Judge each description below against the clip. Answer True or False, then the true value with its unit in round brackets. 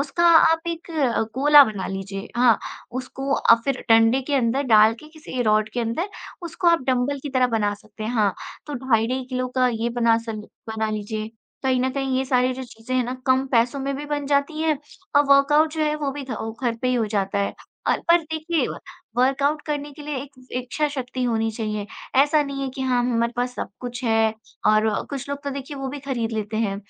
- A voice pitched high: True (255 Hz)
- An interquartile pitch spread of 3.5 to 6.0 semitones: True (4.0 semitones)